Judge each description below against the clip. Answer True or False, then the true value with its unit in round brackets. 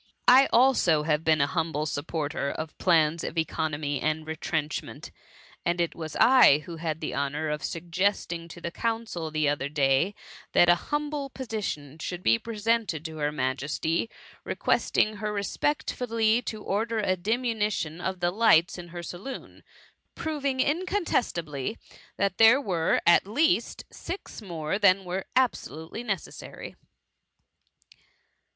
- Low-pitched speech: False (175 Hz)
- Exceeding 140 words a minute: False (135 wpm)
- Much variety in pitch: True (6.2 semitones)